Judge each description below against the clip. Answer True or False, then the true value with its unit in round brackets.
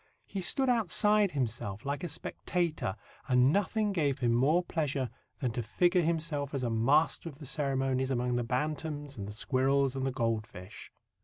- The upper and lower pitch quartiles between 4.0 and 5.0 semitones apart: True (4.7 semitones)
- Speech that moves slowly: False (170 wpm)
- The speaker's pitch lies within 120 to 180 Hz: True (140 Hz)